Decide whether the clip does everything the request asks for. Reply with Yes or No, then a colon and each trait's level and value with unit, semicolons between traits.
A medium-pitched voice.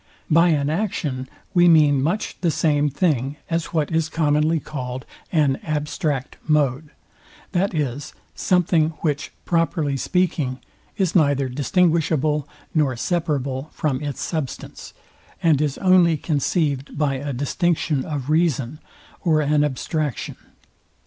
Yes: medium, 150 Hz